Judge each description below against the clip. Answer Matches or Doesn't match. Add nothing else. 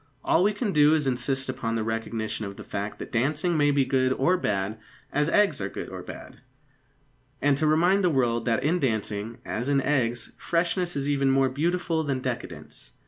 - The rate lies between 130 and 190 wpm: Doesn't match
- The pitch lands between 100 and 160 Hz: Matches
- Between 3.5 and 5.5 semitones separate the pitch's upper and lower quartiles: Matches